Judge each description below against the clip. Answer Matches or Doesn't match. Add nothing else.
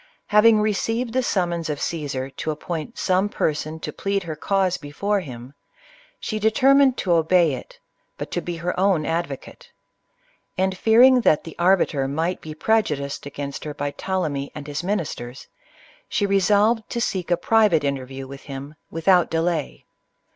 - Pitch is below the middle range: Doesn't match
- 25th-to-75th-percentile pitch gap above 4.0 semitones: Matches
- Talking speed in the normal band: Matches